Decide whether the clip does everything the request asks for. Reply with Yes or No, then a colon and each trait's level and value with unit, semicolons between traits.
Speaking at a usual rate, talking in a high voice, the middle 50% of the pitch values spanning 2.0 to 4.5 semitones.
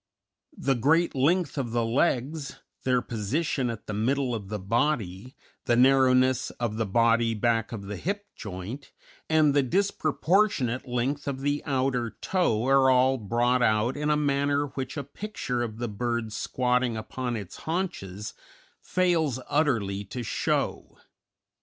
No: average, 145 wpm; low, 125 Hz; average, 3.9 semitones